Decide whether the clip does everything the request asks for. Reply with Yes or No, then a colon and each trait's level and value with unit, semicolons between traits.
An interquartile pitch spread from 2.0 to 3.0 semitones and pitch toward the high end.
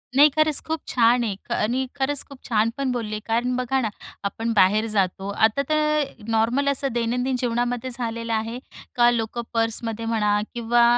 Yes: narrow, 2.6 semitones; high, 235 Hz